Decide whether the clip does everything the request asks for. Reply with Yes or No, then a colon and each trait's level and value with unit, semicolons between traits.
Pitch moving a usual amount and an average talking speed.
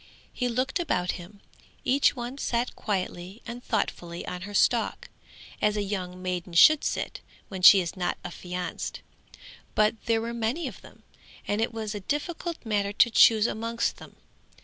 Yes: average, 4.5 semitones; average, 165 wpm